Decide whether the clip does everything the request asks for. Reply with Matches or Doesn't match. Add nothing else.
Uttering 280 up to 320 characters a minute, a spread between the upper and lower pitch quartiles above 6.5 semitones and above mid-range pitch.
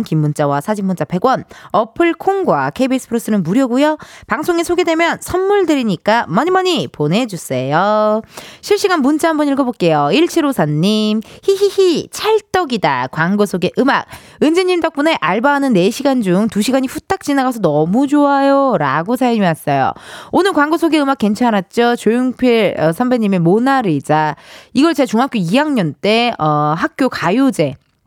Matches